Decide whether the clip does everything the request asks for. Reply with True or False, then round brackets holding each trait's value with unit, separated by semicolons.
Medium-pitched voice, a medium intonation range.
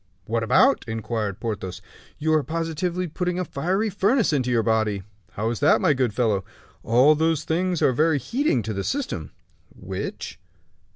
False (145 Hz; 7.8 semitones)